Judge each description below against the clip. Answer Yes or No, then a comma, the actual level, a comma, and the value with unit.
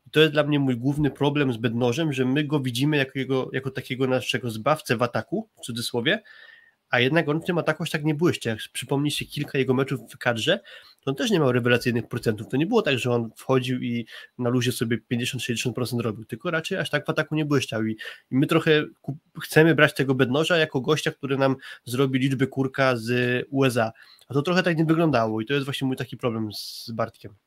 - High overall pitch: No, low, 135 Hz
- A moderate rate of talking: No, fast, 220 wpm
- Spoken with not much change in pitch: No, average, 3.6 semitones